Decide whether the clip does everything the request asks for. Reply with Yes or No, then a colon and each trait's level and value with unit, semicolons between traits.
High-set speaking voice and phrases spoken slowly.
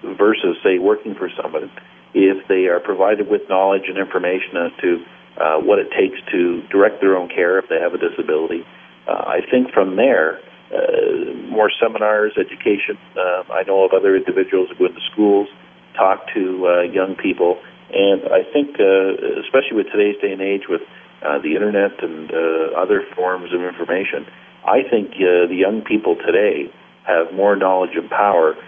No: very high, 360 Hz; average, 180 wpm